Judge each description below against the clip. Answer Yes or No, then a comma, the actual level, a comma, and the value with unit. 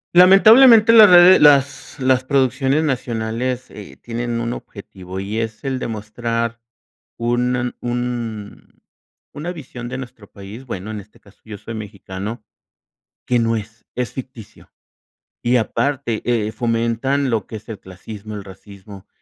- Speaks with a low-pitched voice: Yes, low, 115 Hz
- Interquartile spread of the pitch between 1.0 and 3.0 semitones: No, average, 3.4 semitones